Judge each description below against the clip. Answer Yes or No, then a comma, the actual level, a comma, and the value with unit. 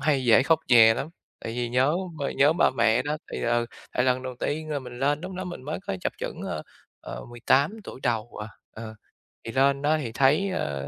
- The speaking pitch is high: No, low, 130 Hz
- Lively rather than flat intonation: No, average, 3.9 semitones